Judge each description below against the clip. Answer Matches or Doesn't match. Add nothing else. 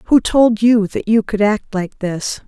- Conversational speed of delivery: Doesn't match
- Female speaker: Matches